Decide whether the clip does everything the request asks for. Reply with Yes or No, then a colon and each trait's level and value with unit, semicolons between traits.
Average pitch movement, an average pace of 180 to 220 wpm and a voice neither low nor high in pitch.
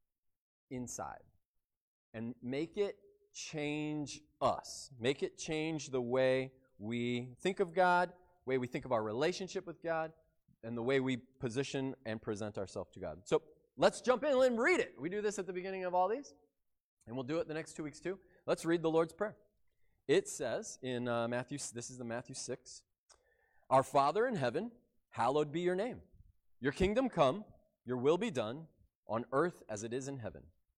No: wide, 6.7 semitones; average, 185 wpm; medium, 145 Hz